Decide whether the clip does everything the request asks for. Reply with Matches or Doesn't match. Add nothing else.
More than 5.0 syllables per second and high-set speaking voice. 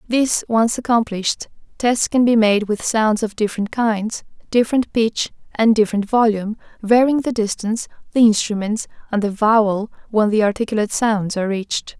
Matches